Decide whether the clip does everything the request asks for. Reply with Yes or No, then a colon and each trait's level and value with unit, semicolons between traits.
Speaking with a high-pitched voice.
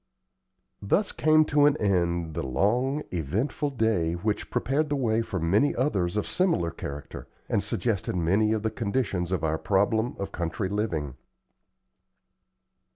No: low, 105 Hz